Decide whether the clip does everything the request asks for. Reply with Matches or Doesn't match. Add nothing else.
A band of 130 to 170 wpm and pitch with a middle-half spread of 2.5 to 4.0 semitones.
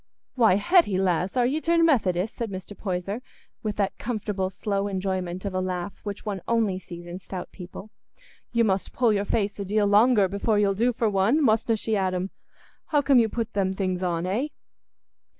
Doesn't match